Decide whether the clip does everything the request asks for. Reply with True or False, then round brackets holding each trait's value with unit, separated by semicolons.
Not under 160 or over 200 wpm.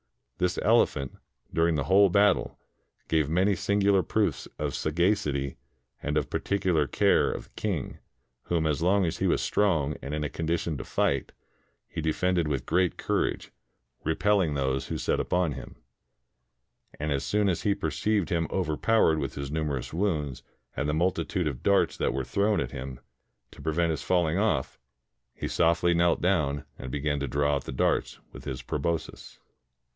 True (175 wpm)